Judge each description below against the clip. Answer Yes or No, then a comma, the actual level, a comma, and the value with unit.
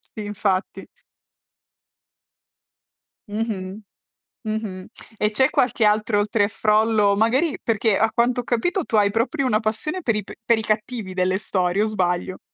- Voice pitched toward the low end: No, high, 215 Hz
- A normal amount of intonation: No, narrow, 2.2 semitones